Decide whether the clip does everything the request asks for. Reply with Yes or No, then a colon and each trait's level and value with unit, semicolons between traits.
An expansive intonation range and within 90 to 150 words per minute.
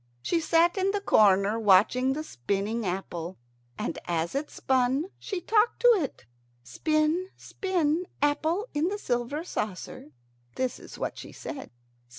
Yes: wide, 8.7 semitones; average, 145 wpm